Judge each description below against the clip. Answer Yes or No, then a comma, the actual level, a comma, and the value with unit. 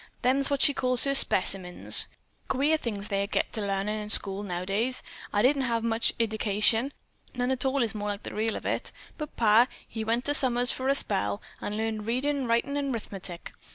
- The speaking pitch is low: No, high, 230 Hz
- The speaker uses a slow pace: No, average, 190 wpm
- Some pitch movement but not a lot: Yes, average, 3.9 semitones